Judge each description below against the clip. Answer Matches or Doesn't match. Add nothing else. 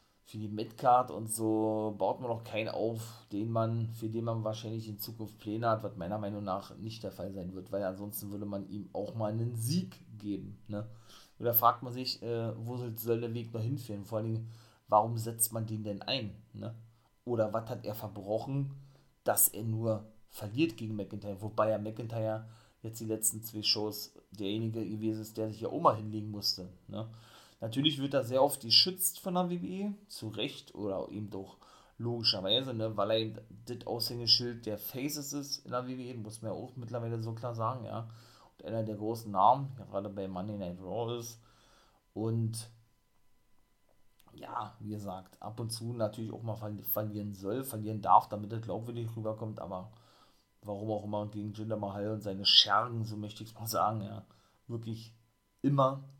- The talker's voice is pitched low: Matches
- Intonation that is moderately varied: Doesn't match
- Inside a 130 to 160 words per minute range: Doesn't match